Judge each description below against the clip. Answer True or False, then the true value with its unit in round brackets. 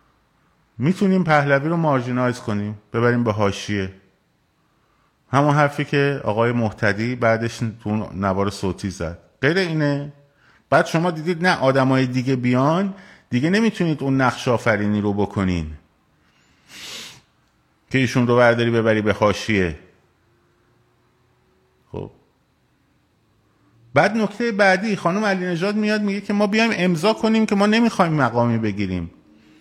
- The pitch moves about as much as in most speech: False (8.2 semitones)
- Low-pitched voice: True (125 Hz)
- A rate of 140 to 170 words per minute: False (120 wpm)